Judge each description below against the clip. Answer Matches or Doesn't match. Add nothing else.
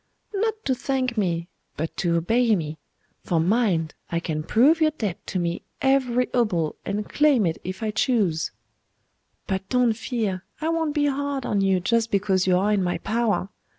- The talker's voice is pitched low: Doesn't match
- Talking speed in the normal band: Matches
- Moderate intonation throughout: Doesn't match